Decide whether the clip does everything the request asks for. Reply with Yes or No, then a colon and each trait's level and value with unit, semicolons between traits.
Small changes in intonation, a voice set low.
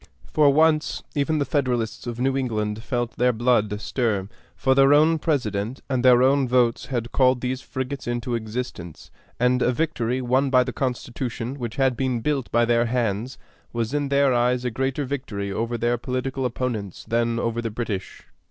Yes: narrow, 2.3 semitones; low, 125 Hz